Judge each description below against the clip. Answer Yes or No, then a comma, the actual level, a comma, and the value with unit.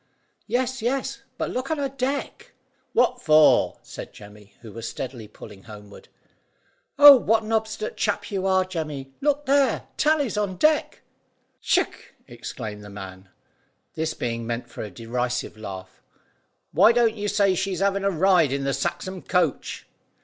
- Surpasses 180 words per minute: No, average, 155 wpm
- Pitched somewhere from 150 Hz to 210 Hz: Yes, medium, 185 Hz